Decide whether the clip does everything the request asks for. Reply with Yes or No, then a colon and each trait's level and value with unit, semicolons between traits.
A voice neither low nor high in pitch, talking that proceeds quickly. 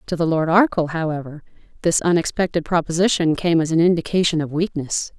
No: medium, 165 Hz; average, 160 wpm